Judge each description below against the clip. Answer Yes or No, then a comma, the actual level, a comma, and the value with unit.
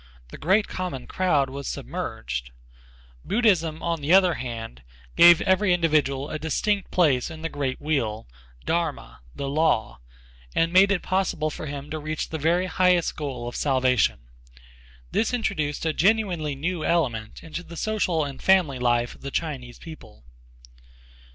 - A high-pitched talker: No, medium, 155 Hz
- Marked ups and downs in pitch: No, average, 4.8 semitones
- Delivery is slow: No, average, 150 wpm